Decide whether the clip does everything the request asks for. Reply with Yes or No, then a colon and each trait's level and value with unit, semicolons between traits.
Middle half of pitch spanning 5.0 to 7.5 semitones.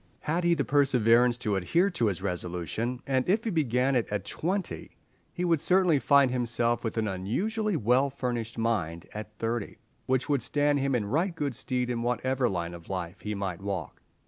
Yes: wide, 5.4 semitones